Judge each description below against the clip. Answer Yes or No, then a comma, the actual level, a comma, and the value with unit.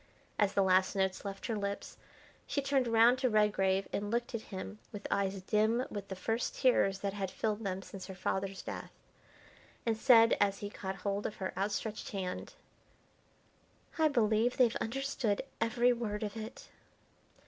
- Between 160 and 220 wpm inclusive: Yes, average, 170 wpm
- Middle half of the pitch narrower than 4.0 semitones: Yes, average, 2.8 semitones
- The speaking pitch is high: Yes, high, 210 Hz